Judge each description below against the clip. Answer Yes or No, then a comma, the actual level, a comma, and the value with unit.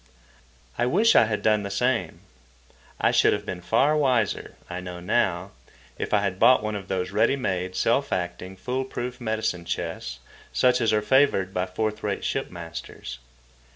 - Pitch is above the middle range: No, low, 105 Hz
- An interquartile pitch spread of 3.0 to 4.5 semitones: No, average, 5.1 semitones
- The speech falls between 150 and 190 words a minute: Yes, average, 175 wpm